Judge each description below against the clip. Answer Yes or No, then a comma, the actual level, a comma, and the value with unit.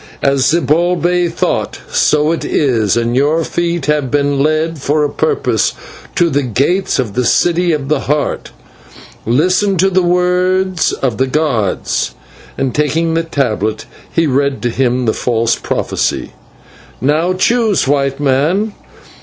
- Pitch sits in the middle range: Yes, medium, 150 Hz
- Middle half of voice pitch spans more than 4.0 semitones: Yes, average, 4.6 semitones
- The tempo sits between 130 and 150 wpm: Yes, average, 145 wpm